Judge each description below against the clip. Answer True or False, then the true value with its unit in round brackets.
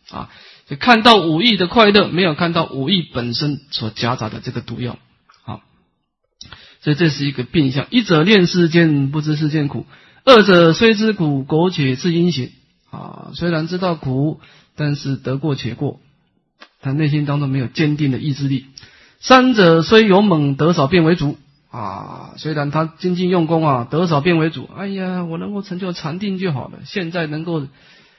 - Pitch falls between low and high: True (160 Hz)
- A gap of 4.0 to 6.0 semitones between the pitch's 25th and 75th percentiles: True (4.4 semitones)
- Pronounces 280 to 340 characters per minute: False (255 characters per minute)